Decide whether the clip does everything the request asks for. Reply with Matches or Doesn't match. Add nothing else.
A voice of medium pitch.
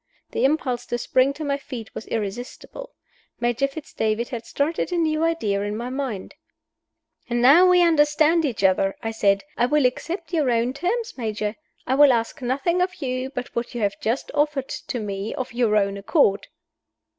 Doesn't match